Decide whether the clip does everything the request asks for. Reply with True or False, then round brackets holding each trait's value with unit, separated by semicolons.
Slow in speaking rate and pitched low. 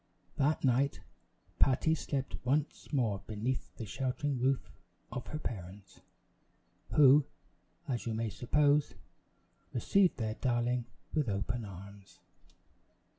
True (110 wpm; 125 Hz)